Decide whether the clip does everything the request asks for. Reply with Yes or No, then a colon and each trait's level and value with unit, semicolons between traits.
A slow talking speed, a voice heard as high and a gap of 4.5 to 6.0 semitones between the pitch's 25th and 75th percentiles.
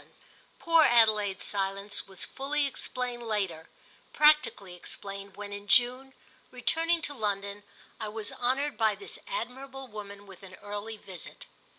Yes: slow, 130 wpm; high, 215 Hz; average, 4.9 semitones